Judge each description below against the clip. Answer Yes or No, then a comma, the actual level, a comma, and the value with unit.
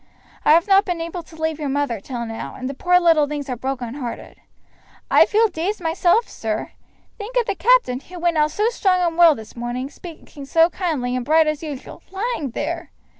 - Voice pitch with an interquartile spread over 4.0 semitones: Yes, average, 5.0 semitones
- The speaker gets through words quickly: Yes, fast, 215 wpm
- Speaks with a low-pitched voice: No, very high, 320 Hz